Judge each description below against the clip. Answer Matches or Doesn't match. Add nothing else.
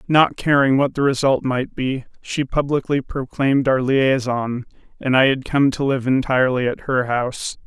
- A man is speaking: Matches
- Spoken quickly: Doesn't match